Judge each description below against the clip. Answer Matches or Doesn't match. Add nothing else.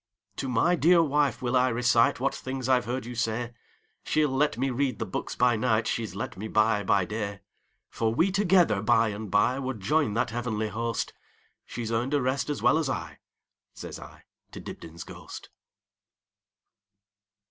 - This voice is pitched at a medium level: Doesn't match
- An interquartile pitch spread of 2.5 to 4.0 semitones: Matches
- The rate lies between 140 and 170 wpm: Matches